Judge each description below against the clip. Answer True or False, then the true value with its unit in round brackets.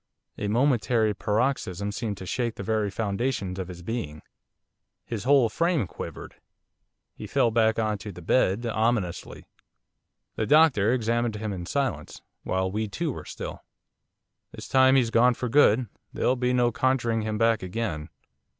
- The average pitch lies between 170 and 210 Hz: False (115 Hz)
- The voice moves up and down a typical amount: True (3.4 semitones)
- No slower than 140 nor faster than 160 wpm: True (155 wpm)